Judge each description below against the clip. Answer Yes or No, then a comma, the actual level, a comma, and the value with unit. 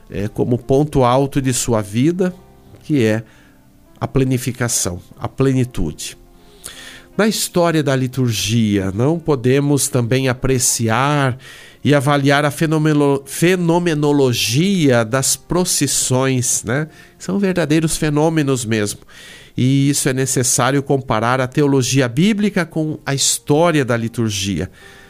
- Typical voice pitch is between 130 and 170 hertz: Yes, low, 135 Hz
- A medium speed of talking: No, slow, 110 wpm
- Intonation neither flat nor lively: Yes, average, 3.9 semitones